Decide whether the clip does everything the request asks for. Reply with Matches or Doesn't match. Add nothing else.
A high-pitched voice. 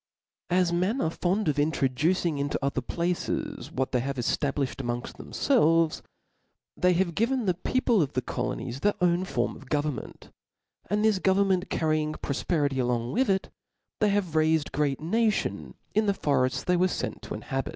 Doesn't match